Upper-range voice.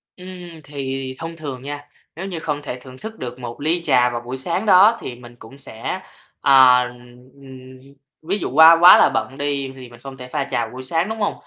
No: low, 135 Hz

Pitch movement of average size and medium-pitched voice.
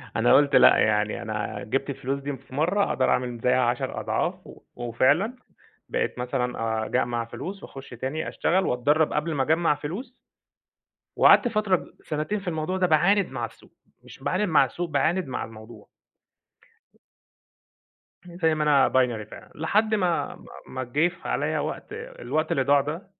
No: wide, 6.2 semitones; medium, 145 Hz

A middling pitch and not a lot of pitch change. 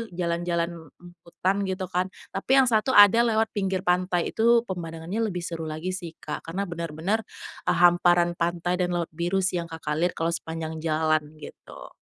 Yes: medium, 175 Hz; narrow, 2.3 semitones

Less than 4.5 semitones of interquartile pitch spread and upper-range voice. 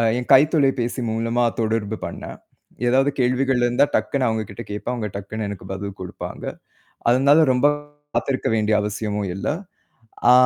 No: average, 3.7 semitones; low, 115 Hz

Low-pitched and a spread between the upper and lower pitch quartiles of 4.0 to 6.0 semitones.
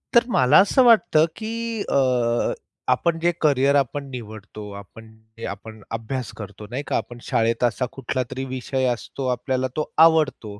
Yes: low, 130 Hz; average, 4.3 semitones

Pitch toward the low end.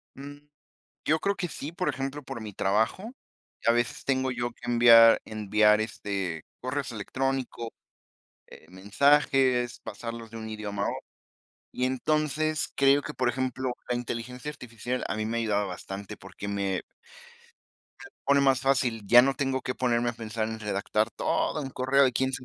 Yes: low, 120 Hz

